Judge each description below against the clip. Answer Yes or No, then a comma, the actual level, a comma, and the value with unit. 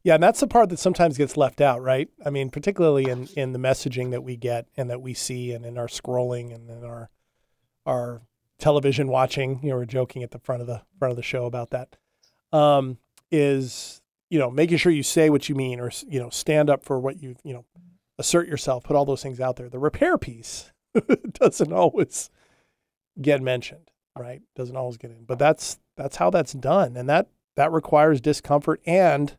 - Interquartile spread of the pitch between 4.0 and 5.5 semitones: No, average, 3.3 semitones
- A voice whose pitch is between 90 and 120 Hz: No, low, 135 Hz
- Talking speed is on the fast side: Yes, fast, 210 wpm